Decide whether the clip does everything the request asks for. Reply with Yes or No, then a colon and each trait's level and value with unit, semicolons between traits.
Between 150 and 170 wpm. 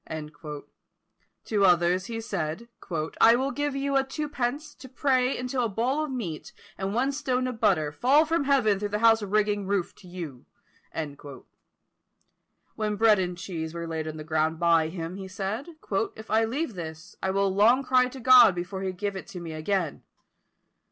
No: average, 180 wpm